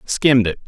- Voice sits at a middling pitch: No, low, 120 Hz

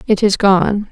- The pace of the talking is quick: No, average, 195 wpm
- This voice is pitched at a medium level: No, high, 200 Hz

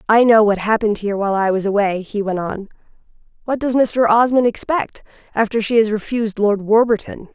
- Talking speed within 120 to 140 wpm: No, average, 190 wpm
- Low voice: No, high, 215 Hz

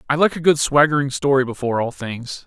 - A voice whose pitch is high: No, medium, 140 Hz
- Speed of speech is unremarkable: No, fast, 220 wpm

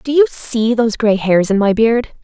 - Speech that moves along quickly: Yes, fast, 240 wpm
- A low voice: No, high, 225 Hz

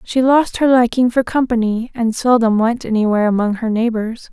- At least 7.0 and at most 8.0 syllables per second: No, 5.3 syllables/s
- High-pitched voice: Yes, high, 235 Hz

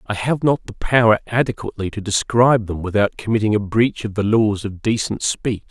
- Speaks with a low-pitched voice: Yes, low, 110 Hz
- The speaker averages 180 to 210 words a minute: Yes, average, 200 wpm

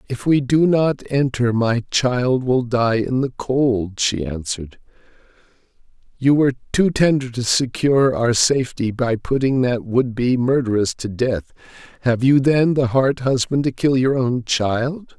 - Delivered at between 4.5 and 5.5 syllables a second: No, 4.2 syllables/s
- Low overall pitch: Yes, low, 125 Hz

